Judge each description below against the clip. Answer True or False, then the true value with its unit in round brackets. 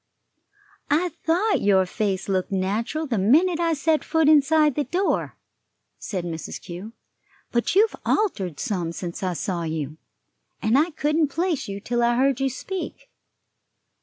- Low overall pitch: False (245 Hz)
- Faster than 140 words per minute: True (150 wpm)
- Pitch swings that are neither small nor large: False (9.0 semitones)